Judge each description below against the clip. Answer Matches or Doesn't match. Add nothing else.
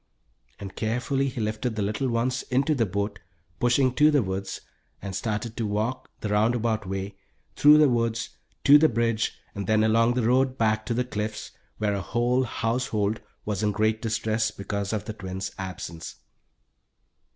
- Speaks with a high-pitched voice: Doesn't match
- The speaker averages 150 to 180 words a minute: Matches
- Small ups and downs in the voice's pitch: Doesn't match